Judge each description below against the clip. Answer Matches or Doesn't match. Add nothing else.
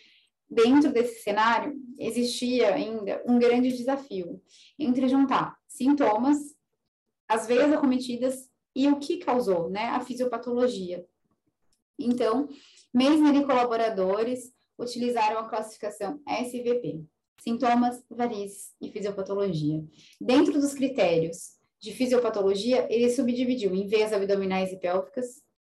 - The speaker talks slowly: Matches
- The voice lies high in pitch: Matches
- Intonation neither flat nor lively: Matches